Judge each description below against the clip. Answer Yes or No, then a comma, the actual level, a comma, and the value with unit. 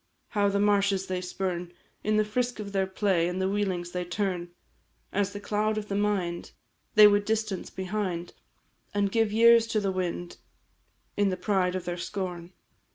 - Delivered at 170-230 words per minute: Yes, average, 175 wpm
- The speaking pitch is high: Yes, high, 195 Hz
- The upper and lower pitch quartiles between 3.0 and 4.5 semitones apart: No, narrow, 2.4 semitones